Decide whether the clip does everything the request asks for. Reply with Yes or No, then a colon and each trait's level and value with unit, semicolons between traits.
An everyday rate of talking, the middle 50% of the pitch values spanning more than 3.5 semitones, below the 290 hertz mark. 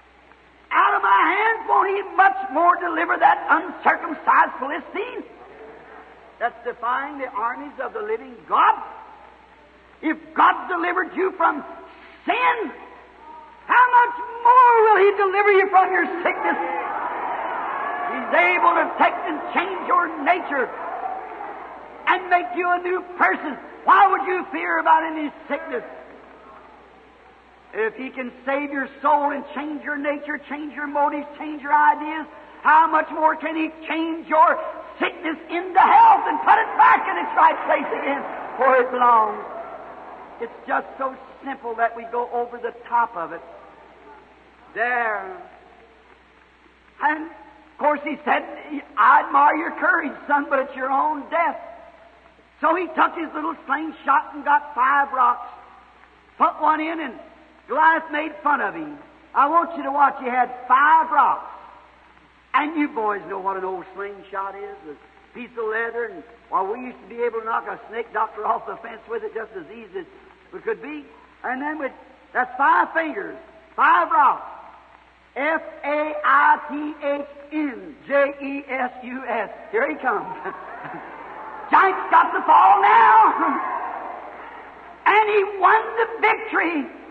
No: average, 145 wpm; average, 5.1 semitones; very high, 310 Hz